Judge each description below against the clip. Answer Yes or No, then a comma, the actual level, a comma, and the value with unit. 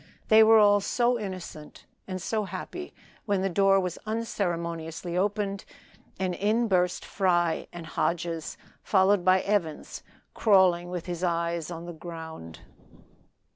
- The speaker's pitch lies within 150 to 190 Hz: Yes, medium, 185 Hz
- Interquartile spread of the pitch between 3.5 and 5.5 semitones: No, average, 3.0 semitones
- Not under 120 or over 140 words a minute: Yes, slow, 135 wpm